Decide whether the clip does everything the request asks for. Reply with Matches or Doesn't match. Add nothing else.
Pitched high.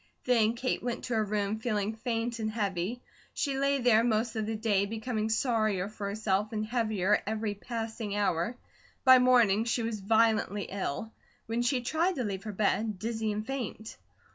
Matches